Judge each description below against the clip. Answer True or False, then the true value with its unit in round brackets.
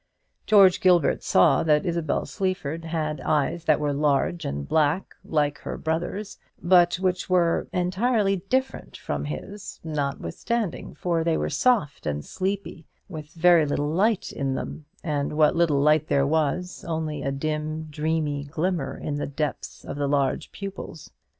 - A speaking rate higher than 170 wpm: False (150 wpm)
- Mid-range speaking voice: True (160 Hz)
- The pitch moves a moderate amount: True (3.7 semitones)